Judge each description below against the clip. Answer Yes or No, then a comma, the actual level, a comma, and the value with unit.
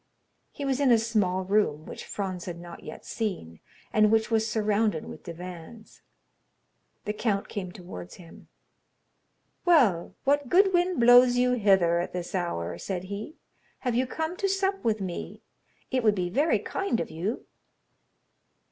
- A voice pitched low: No, high, 215 Hz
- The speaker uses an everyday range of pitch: No, wide, 5.8 semitones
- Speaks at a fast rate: No, average, 155 wpm